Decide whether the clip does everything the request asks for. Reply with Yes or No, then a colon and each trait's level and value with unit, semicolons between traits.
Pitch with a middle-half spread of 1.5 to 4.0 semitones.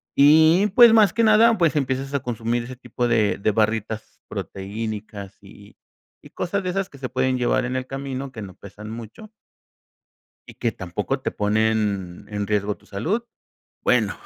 No: average, 5.3 semitones